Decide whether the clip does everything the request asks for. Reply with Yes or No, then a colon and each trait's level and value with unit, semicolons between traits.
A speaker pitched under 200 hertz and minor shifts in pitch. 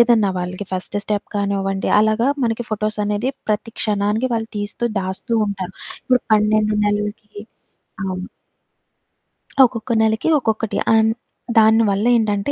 No: high, 215 Hz; narrow, 1.7 semitones